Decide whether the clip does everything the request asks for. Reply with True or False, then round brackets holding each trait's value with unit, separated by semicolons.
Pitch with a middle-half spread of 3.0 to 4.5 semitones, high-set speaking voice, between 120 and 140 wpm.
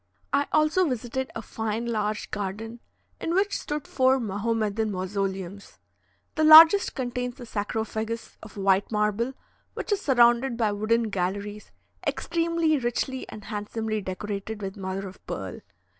True (4.2 semitones; 220 Hz; 135 wpm)